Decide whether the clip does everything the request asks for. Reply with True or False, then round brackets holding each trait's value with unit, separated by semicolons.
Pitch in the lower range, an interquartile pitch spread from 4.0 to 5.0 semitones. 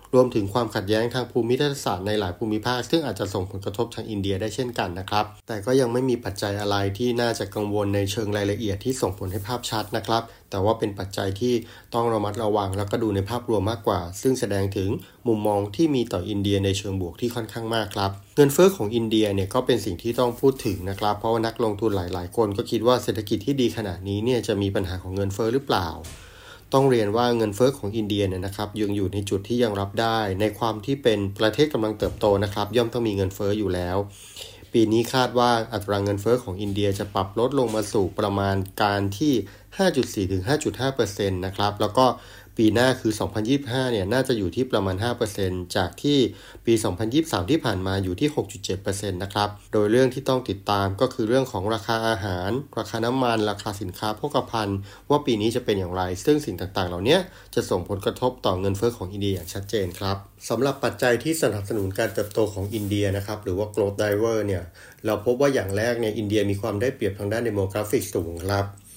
False (105 Hz; 3.2 semitones)